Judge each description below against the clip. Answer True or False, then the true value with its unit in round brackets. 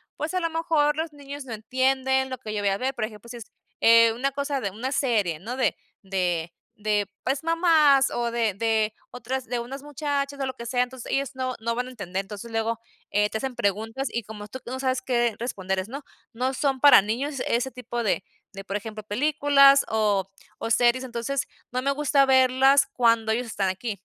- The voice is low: False (245 Hz)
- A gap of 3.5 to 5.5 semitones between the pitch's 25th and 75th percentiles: True (3.8 semitones)